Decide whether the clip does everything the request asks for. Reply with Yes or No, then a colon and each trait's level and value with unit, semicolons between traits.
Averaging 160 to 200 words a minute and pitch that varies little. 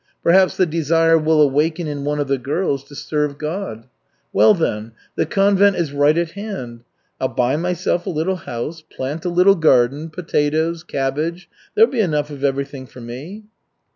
No: average, 170 wpm; average, 3.9 semitones